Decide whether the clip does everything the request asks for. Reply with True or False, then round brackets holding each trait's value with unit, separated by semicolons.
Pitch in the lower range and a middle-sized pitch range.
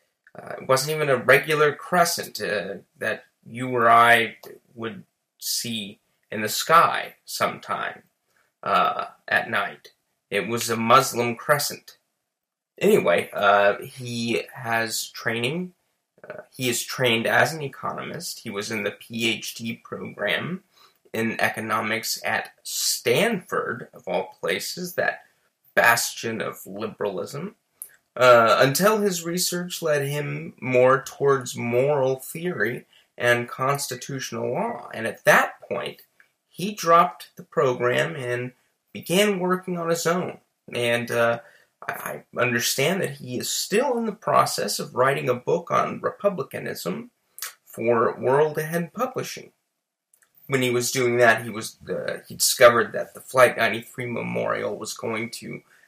False (125 Hz; 6.2 semitones)